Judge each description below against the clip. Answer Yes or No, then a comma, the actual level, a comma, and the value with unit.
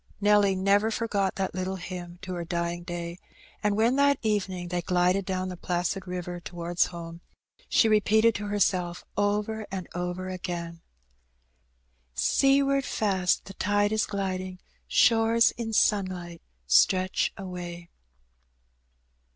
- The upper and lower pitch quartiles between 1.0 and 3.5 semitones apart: Yes, average, 2.9 semitones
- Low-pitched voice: No, medium, 185 Hz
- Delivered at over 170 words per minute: No, slow, 135 wpm